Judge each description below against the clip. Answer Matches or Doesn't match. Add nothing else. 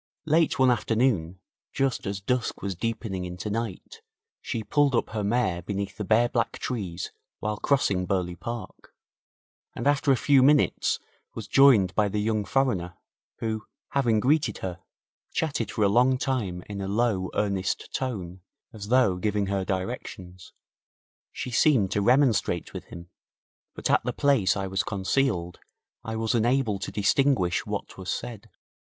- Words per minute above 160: Doesn't match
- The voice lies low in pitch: Matches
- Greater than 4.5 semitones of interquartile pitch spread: Matches